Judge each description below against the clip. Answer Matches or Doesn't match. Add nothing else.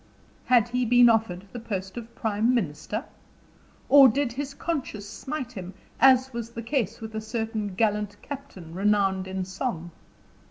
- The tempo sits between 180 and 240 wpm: Doesn't match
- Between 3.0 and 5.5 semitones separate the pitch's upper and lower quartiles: Matches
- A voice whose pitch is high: Matches